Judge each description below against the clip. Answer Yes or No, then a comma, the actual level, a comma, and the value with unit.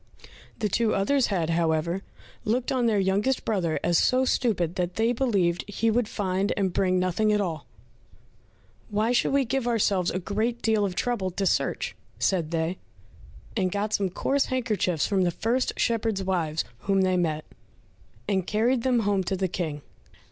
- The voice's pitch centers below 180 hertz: No, high, 200 Hz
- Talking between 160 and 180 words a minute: Yes, average, 170 wpm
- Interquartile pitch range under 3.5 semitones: No, average, 4.1 semitones